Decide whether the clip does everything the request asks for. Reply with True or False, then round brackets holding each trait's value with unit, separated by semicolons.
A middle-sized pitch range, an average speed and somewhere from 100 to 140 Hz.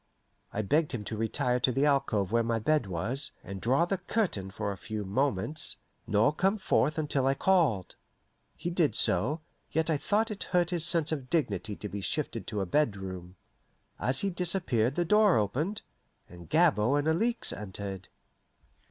False (8.0 semitones; 175 wpm; 135 Hz)